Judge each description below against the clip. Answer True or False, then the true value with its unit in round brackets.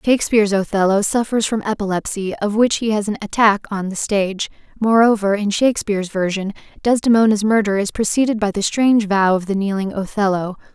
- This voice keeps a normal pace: True (165 wpm)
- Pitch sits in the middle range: False (205 Hz)